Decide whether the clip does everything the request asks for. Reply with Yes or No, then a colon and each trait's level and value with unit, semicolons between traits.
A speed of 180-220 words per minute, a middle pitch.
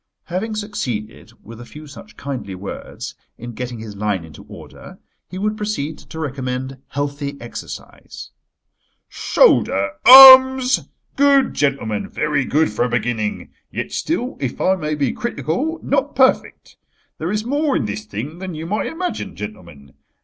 No: average, 150 wpm; medium, 145 Hz